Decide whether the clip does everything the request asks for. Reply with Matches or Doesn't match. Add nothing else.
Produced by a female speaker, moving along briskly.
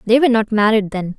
Matches